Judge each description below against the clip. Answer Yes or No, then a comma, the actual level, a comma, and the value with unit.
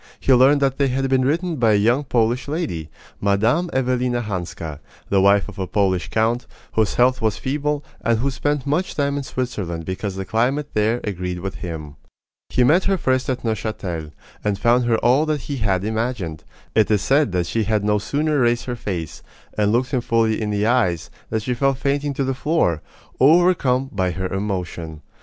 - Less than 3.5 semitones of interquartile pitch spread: No, average, 5.2 semitones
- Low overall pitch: Yes, low, 115 Hz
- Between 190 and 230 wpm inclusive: Yes, average, 195 wpm